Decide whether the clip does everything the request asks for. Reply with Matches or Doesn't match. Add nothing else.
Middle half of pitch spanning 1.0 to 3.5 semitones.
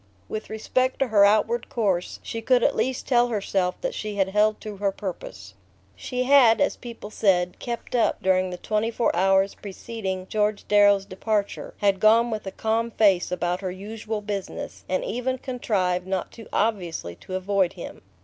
Matches